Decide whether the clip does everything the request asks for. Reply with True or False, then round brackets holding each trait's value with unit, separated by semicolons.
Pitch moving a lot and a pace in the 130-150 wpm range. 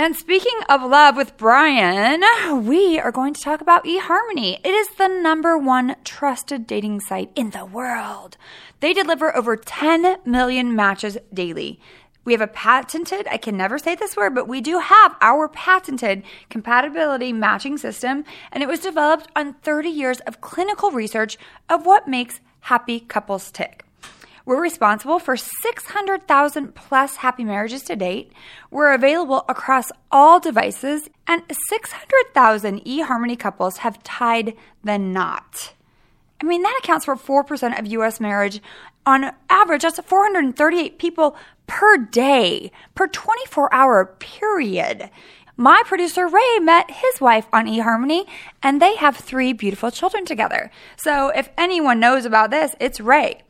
True (6.3 semitones; 145 wpm)